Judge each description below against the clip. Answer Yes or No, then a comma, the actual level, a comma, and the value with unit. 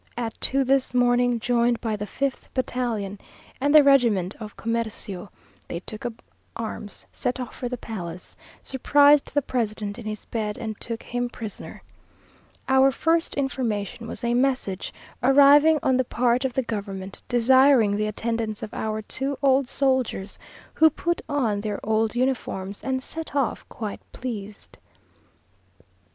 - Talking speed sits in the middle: Yes, average, 150 wpm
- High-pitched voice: Yes, high, 240 Hz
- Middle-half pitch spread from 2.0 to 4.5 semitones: Yes, average, 3.7 semitones